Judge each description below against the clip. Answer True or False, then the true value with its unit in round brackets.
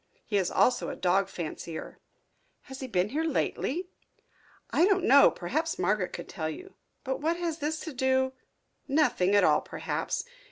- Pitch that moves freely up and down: True (8.5 semitones)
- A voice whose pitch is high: True (260 Hz)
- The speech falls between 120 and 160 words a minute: False (170 wpm)